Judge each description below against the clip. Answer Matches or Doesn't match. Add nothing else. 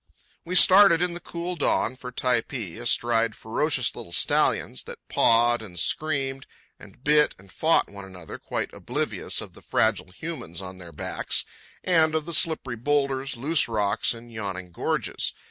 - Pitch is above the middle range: Doesn't match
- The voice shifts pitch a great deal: Matches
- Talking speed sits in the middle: Matches